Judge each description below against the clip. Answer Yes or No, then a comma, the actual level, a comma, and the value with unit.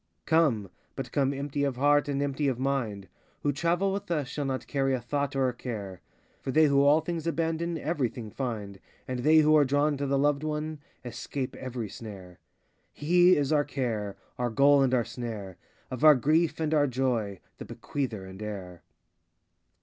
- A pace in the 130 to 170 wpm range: No, average, 185 wpm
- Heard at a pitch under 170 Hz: Yes, low, 135 Hz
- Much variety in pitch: No, average, 4.0 semitones